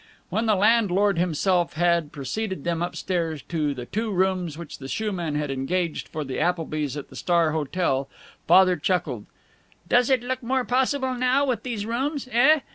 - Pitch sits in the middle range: Yes, medium, 180 Hz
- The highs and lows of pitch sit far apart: Yes, wide, 6.8 semitones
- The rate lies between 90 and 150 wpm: No, average, 175 wpm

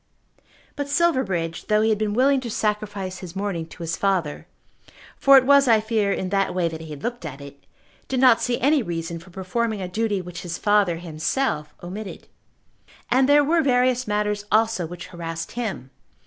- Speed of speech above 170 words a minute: Yes, average, 190 wpm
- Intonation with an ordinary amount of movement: No, wide, 5.9 semitones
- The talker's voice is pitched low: No, high, 205 Hz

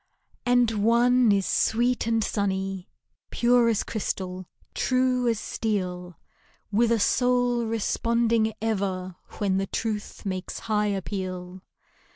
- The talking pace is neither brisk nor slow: No, slow, 115 wpm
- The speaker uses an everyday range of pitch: Yes, average, 3.5 semitones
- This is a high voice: Yes, high, 220 Hz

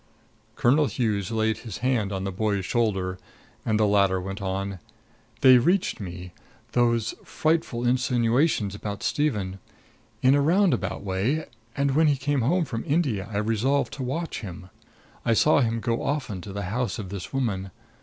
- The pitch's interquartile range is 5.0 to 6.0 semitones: Yes, wide, 5.5 semitones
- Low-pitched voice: Yes, low, 115 Hz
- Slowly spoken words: No, average, 165 wpm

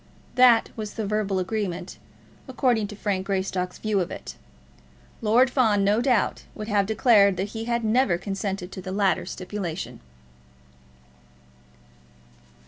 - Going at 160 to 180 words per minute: No, slow, 135 wpm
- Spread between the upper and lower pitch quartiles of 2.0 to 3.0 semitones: Yes, average, 2.7 semitones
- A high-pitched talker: Yes, high, 205 Hz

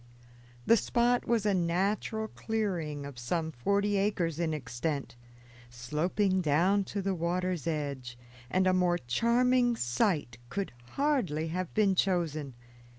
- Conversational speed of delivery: No, slow, 130 wpm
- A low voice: No, medium, 180 Hz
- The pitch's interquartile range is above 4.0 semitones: Yes, average, 5.2 semitones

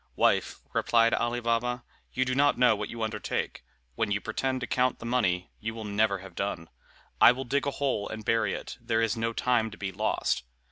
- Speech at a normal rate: No, fast, 215 wpm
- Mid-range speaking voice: No, low, 115 Hz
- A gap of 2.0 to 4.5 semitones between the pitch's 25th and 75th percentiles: Yes, average, 2.9 semitones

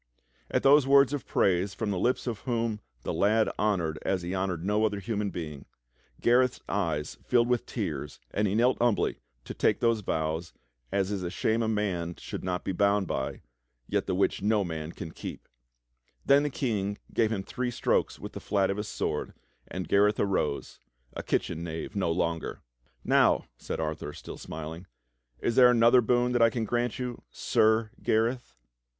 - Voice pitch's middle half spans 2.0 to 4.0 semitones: No, average, 4.8 semitones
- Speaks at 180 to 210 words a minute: Yes, average, 190 wpm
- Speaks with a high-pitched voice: No, low, 105 Hz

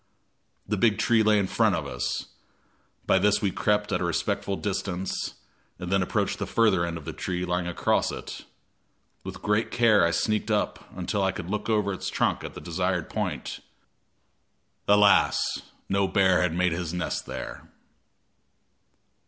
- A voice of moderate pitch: No, very low, 95 Hz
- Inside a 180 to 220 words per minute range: No, average, 165 wpm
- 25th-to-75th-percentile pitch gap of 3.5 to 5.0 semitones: No, average, 2.8 semitones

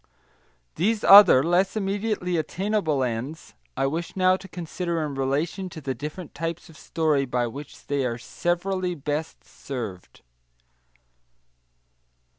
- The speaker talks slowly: Yes, slow, 125 wpm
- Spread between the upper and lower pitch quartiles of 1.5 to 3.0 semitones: No, average, 5.0 semitones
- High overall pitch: No, medium, 160 Hz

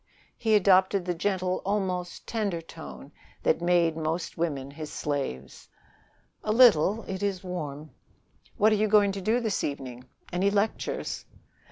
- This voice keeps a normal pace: Yes, average, 145 wpm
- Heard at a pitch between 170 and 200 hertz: Yes, medium, 185 Hz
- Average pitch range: Yes, average, 4.5 semitones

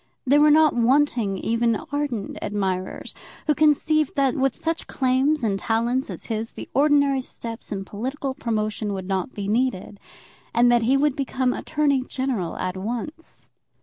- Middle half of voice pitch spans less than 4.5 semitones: No, average, 4.8 semitones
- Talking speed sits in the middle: Yes, average, 160 wpm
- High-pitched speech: Yes, very high, 250 Hz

